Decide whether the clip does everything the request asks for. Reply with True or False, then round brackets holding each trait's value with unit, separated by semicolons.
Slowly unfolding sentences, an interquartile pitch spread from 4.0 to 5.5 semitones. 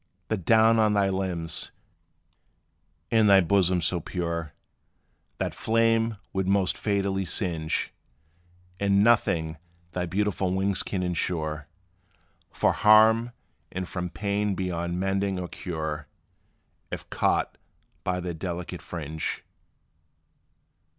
False (110 wpm; 2.8 semitones)